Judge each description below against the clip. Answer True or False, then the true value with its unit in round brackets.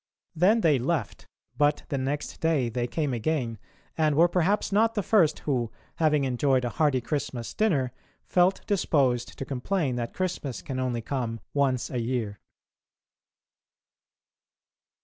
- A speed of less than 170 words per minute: True (140 wpm)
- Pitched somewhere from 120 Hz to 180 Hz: True (140 Hz)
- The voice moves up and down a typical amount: True (4.8 semitones)